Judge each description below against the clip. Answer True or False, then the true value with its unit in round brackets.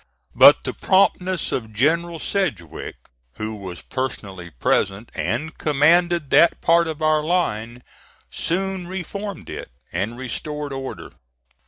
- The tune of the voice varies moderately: False (7.3 semitones)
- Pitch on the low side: False (150 Hz)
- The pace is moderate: False (120 wpm)